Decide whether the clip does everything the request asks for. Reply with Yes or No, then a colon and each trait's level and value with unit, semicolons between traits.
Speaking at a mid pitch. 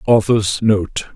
No: low, 105 Hz